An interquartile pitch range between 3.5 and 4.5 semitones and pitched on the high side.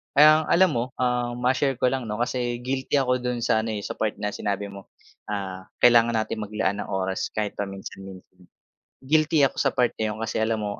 No: average, 3.8 semitones; low, 115 Hz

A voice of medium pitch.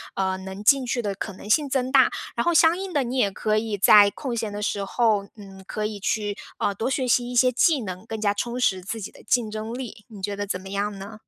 No: high, 215 Hz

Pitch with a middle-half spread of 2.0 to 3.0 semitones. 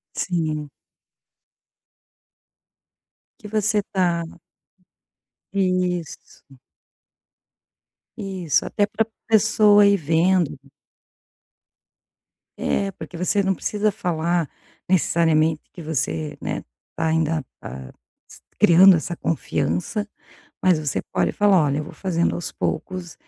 No: average, 3.7 semitones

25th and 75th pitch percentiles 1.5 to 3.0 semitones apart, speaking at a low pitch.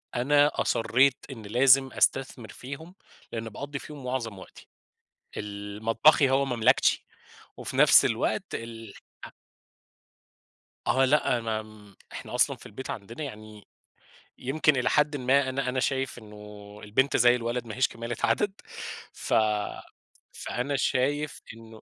No: average, 3.4 semitones; low, 125 Hz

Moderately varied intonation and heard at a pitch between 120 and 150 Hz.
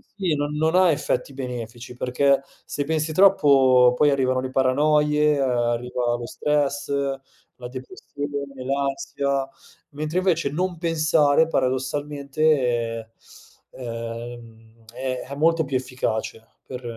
Yes: average, 3.2 semitones; low, 135 Hz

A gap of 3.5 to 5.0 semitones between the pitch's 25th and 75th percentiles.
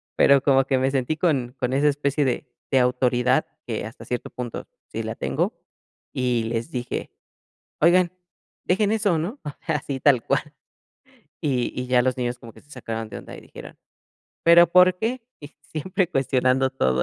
Yes: average, 4.1 semitones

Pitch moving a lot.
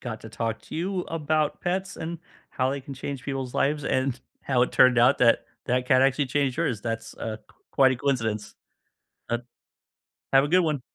No: average, 3.2 semitones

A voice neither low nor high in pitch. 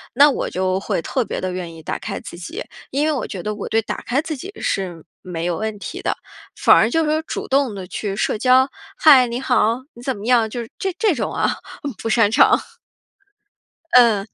No: high, 230 Hz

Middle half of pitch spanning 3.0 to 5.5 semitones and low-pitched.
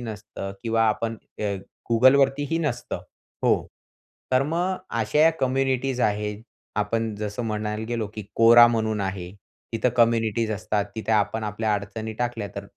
No: narrow, 2.5 semitones; low, 110 Hz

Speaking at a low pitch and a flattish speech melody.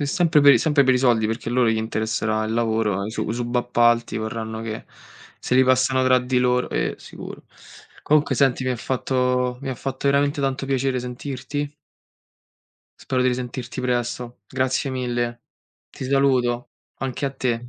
Yes: low, 125 Hz; narrow, 1.9 semitones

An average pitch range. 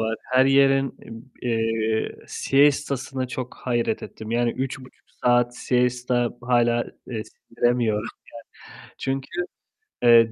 No: narrow, 2.0 semitones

